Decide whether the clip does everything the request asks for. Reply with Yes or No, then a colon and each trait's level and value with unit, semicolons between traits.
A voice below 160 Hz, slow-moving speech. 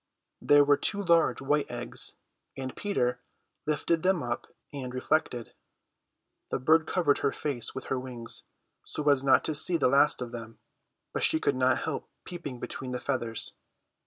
No: medium, 140 Hz; average, 165 wpm